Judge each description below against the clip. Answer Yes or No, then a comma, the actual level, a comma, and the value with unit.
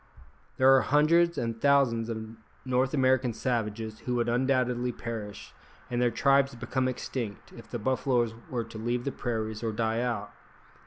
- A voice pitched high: No, low, 120 Hz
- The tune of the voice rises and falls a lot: No, narrow, 2.5 semitones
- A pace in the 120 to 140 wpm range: No, average, 160 wpm